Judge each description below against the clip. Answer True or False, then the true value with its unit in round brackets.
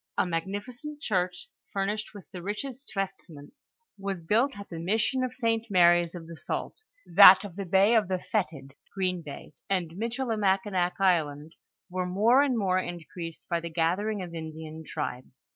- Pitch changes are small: False (4.3 semitones)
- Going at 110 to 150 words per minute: False (160 wpm)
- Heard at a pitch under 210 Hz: True (190 Hz)